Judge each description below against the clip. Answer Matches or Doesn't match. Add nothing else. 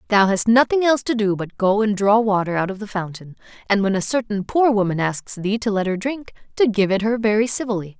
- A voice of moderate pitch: Doesn't match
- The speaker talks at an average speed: Doesn't match